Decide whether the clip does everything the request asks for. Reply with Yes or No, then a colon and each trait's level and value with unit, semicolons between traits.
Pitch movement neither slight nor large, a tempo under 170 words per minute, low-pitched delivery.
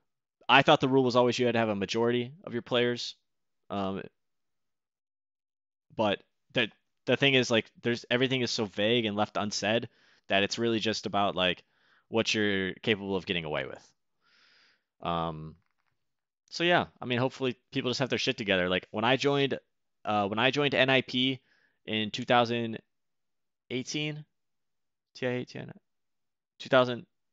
Yes: average, 3.6 semitones; average, 160 wpm; low, 120 Hz